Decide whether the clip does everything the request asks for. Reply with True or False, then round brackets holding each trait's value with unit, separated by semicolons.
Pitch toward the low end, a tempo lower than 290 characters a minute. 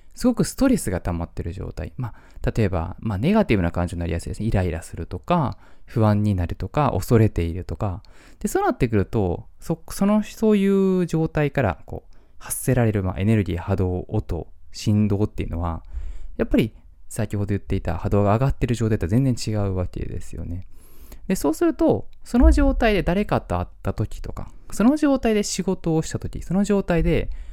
False (105 Hz; 385 characters per minute)